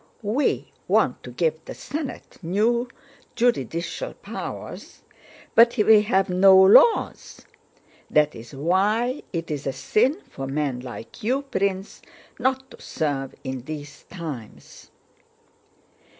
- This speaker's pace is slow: Yes, slow, 120 wpm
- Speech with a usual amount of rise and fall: No, wide, 8.3 semitones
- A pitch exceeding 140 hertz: Yes, high, 190 Hz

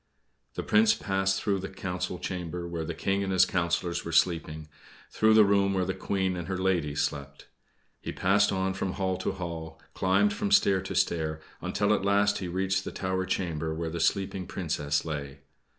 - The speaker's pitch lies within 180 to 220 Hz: No, very low, 95 Hz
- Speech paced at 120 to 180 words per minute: No, average, 190 wpm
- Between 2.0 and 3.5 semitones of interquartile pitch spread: Yes, narrow, 2.6 semitones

